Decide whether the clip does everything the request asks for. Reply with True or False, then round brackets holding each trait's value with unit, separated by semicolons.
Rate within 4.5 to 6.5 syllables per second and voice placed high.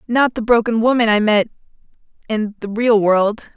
True (4.8 syllables/s; 220 Hz)